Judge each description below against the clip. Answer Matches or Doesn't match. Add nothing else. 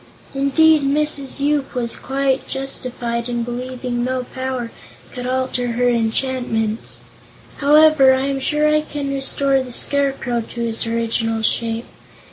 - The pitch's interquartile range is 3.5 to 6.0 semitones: Doesn't match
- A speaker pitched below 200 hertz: Doesn't match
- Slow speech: Matches